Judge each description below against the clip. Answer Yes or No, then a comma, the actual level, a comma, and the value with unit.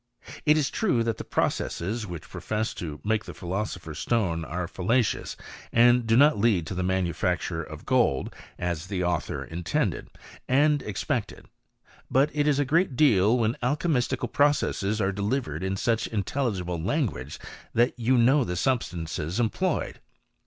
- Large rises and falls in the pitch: Yes, wide, 6.2 semitones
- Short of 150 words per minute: No, average, 155 wpm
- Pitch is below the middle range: Yes, low, 110 Hz